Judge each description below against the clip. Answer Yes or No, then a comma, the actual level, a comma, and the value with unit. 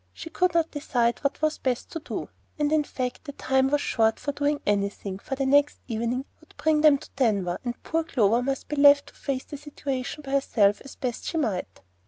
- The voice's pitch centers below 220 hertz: No, very high, 275 Hz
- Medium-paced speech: No, fast, 220 wpm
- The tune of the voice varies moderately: Yes, average, 3.6 semitones